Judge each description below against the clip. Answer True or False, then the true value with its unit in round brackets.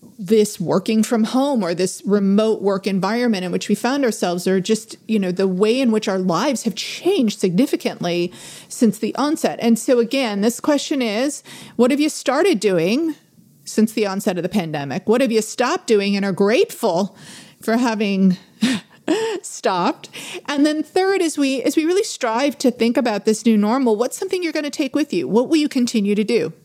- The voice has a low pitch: False (230 Hz)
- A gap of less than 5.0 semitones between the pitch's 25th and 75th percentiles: False (5.3 semitones)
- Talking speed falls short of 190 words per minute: False (195 wpm)